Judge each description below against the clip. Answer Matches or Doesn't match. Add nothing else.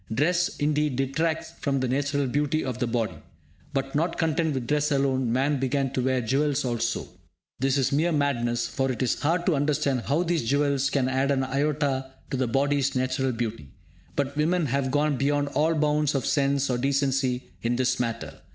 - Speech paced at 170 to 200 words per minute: Matches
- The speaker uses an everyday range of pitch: Doesn't match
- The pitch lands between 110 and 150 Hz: Matches